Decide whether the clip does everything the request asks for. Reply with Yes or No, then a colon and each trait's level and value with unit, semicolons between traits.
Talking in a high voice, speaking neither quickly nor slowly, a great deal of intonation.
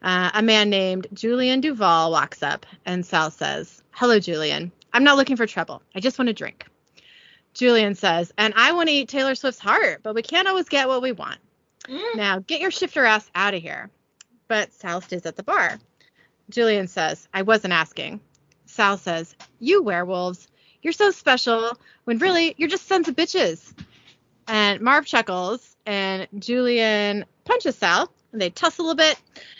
Yes: high, 225 Hz; average, 175 wpm; wide, 6.2 semitones